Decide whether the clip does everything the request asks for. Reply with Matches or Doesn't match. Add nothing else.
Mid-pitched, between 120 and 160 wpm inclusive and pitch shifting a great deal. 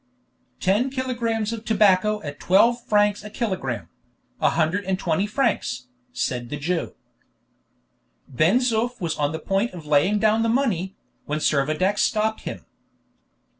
Doesn't match